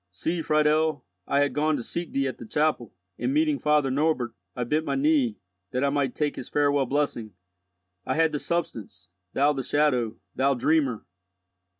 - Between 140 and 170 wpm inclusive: No, average, 180 wpm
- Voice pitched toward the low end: No, medium, 145 Hz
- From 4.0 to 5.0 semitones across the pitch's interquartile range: No, average, 3.3 semitones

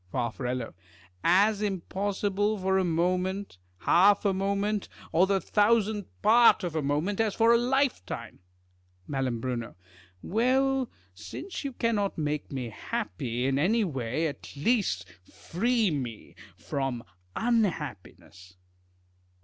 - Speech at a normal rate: No, slow, 115 wpm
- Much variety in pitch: Yes, wide, 7.5 semitones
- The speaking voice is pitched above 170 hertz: Yes, high, 190 Hz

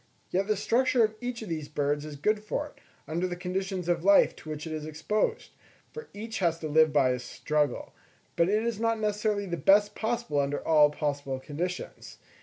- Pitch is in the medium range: Yes, medium, 180 Hz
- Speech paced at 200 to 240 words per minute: Yes, fast, 205 wpm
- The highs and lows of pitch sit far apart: Yes, wide, 5.9 semitones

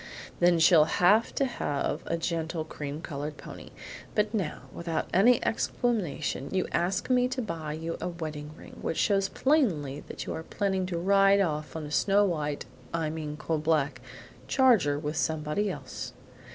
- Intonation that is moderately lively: Yes, average, 4.6 semitones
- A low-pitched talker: No, medium, 165 Hz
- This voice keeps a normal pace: Yes, average, 165 wpm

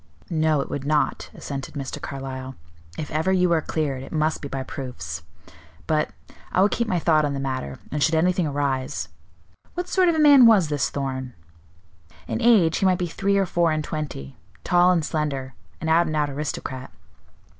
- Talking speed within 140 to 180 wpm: No, average, 190 wpm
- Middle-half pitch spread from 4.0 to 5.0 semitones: Yes, average, 4.4 semitones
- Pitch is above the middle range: No, medium, 155 Hz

